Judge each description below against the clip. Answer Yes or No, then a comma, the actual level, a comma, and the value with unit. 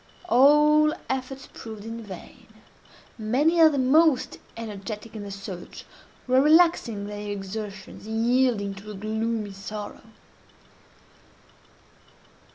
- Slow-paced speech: Yes, slow, 110 wpm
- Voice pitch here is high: Yes, high, 225 Hz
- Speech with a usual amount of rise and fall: Yes, average, 4.4 semitones